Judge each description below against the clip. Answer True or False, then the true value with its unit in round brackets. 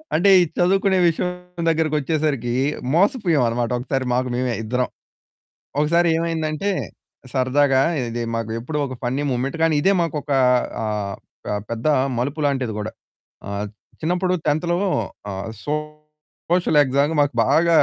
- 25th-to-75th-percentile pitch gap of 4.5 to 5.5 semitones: True (4.8 semitones)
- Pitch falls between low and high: True (150 Hz)